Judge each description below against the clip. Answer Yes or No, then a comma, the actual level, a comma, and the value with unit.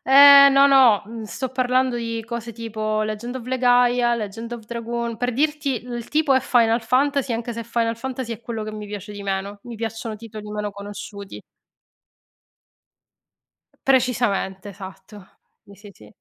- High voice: Yes, high, 230 Hz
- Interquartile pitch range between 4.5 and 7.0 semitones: No, average, 2.8 semitones